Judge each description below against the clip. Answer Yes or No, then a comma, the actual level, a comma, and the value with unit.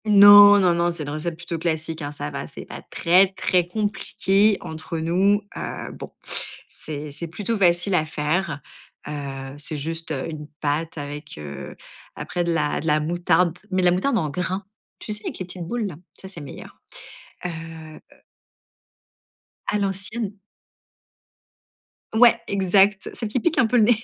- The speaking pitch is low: No, medium, 175 Hz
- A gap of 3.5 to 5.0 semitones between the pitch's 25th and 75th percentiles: Yes, average, 4.2 semitones